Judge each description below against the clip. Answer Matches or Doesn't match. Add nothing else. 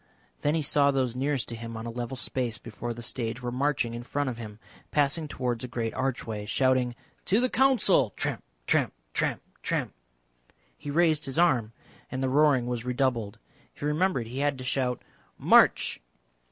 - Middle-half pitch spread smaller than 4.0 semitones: Matches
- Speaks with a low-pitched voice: Matches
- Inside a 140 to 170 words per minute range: Doesn't match